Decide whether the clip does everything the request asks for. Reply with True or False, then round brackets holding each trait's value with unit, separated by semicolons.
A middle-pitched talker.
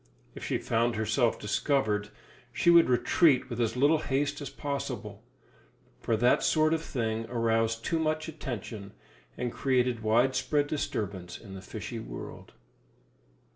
False (120 Hz)